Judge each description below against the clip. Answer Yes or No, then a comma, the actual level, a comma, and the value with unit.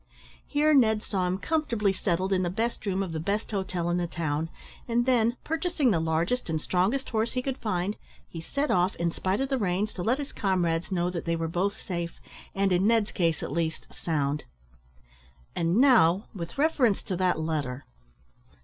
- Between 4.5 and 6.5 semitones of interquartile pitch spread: Yes, average, 5.3 semitones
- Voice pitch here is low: No, high, 190 Hz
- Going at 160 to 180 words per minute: No, average, 195 wpm